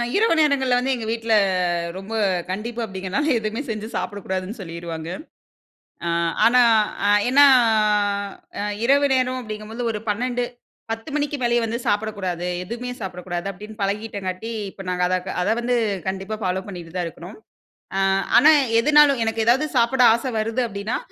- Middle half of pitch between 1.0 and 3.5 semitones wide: No, average, 4.4 semitones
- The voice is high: Yes, high, 220 Hz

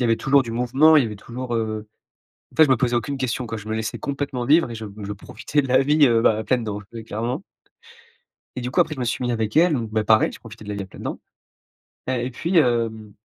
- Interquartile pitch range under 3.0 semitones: No, average, 3.3 semitones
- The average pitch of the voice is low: Yes, low, 120 Hz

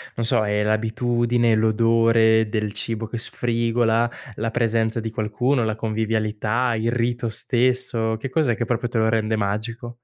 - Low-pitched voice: Yes, low, 115 Hz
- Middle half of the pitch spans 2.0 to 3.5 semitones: No, narrow, 1.3 semitones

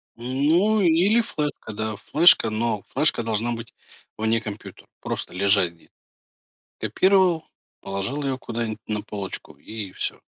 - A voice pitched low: Yes, low, 115 Hz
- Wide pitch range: Yes, wide, 6.3 semitones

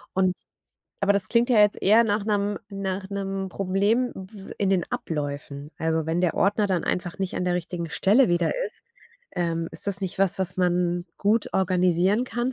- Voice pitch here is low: No, high, 190 Hz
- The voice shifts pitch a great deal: No, narrow, 2.5 semitones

